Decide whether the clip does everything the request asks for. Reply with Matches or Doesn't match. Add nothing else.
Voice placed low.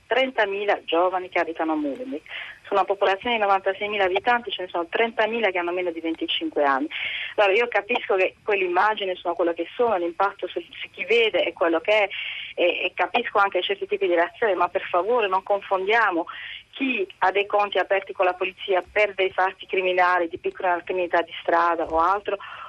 Doesn't match